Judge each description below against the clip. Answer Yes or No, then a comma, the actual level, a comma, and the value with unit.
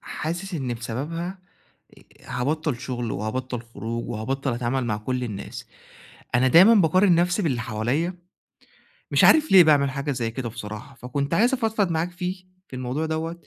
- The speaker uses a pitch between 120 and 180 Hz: Yes, medium, 140 Hz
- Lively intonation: Yes, wide, 6.1 semitones